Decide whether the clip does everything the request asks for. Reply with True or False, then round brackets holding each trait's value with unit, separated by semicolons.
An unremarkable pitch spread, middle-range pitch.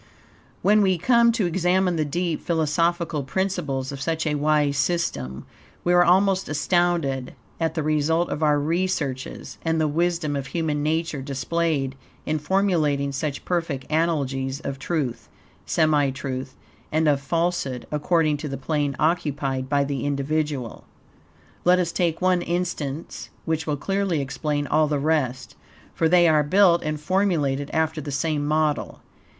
True (3.4 semitones; 155 Hz)